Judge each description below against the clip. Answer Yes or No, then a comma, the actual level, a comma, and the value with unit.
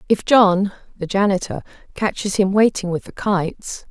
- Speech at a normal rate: No, slow, 125 wpm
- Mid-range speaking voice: No, high, 195 Hz